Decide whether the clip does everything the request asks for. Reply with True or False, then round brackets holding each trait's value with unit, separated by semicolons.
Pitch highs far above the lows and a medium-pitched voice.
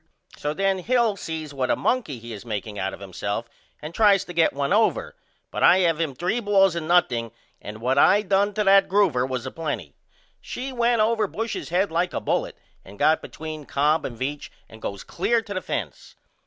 True (7.7 semitones; 165 Hz)